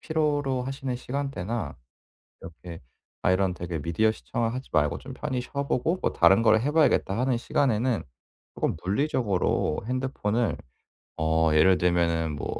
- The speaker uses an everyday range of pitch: No, wide, 7.2 semitones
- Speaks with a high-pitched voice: No, low, 115 Hz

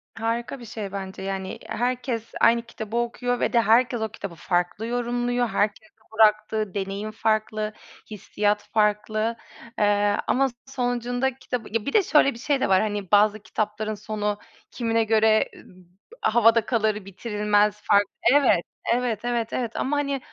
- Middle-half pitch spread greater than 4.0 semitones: No, narrow, 2.6 semitones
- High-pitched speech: Yes, high, 220 Hz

